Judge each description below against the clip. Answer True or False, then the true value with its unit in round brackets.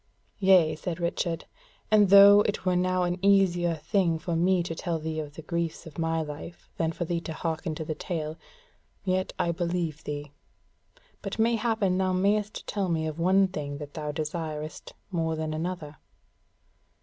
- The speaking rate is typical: True (175 wpm)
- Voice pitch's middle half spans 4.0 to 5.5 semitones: False (2.9 semitones)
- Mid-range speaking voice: True (170 Hz)